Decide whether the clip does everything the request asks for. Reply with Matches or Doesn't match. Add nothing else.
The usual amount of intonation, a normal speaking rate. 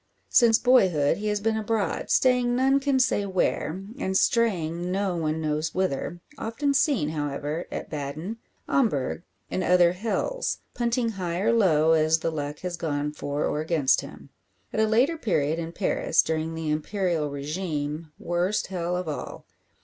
Doesn't match